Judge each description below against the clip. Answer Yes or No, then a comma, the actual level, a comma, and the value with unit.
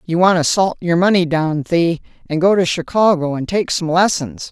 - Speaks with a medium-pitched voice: Yes, medium, 170 Hz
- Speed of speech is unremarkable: No, fast, 210 wpm